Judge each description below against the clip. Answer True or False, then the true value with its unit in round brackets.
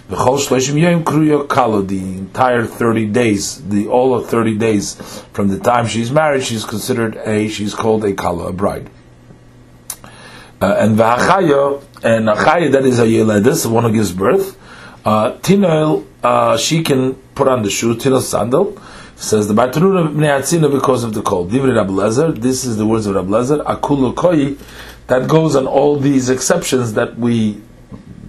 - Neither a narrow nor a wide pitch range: True (4.7 semitones)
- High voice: False (115 Hz)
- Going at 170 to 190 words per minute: False (155 wpm)